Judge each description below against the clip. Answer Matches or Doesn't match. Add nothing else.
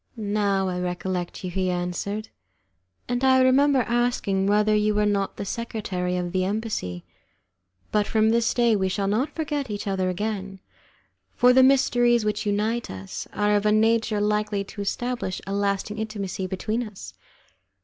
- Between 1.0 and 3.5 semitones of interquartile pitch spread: Matches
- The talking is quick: Doesn't match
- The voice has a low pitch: Doesn't match